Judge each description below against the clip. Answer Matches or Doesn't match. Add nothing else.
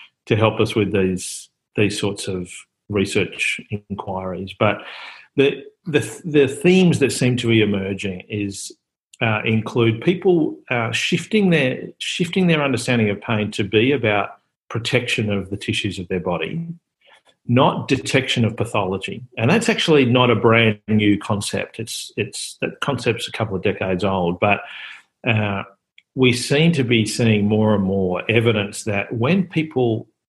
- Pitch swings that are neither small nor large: Matches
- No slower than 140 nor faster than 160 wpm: Matches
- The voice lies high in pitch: Doesn't match